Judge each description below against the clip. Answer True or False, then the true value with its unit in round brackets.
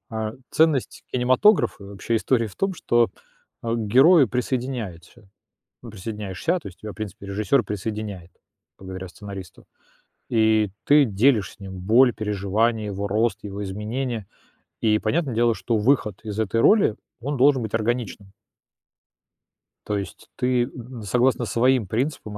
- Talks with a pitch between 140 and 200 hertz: False (110 Hz)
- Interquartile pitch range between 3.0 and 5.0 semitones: True (3.6 semitones)